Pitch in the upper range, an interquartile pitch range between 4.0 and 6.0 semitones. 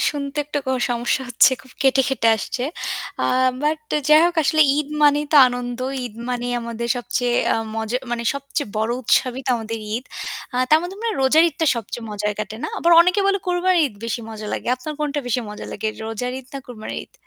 Yes: very high, 255 Hz; average, 4.3 semitones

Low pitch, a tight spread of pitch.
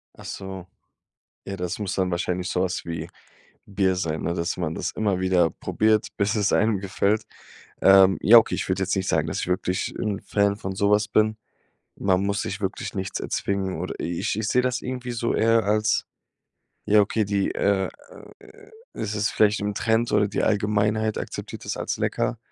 Yes: low, 100 Hz; narrow, 2.3 semitones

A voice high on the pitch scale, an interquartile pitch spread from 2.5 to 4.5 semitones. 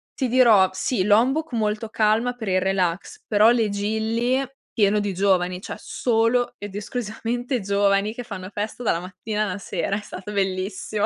Yes: high, 210 Hz; average, 2.8 semitones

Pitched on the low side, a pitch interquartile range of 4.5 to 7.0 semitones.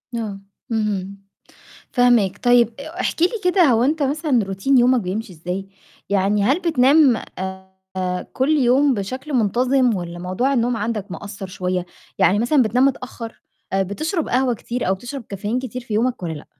No: high, 235 Hz; average, 5.1 semitones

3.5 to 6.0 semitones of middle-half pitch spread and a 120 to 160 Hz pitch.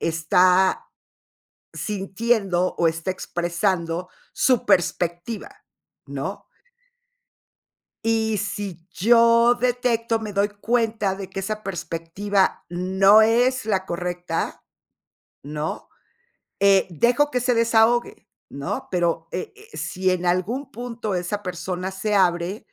No: average, 4.3 semitones; high, 195 Hz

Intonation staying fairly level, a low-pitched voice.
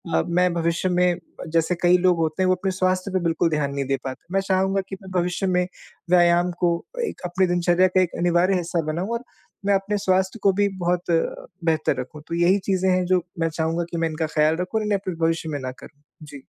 No: narrow, 2.2 semitones; medium, 175 Hz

